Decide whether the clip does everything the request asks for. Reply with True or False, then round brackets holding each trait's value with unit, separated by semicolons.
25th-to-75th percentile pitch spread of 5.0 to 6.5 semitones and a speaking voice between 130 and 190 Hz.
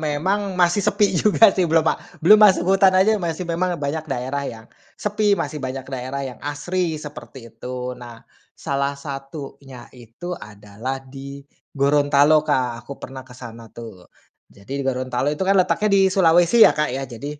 True (5.3 semitones; 140 Hz)